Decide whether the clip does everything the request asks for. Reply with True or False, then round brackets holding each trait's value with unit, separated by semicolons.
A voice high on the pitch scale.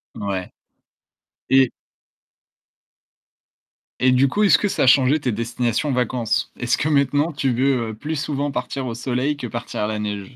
False (125 Hz)